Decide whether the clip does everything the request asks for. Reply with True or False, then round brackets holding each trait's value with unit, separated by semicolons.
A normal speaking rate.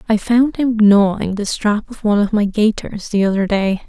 False (215 wpm)